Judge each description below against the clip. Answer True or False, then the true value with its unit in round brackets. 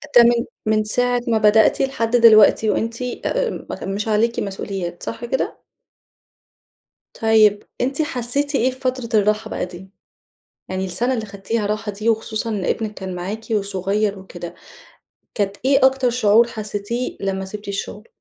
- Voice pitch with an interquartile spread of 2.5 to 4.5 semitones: True (3.0 semitones)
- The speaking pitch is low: False (215 Hz)